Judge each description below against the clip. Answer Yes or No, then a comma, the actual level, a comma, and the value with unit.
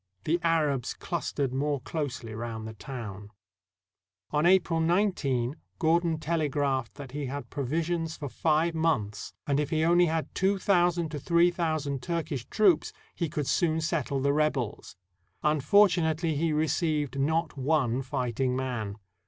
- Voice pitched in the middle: Yes, medium, 150 Hz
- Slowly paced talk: No, average, 145 wpm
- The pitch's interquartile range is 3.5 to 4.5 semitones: Yes, average, 3.8 semitones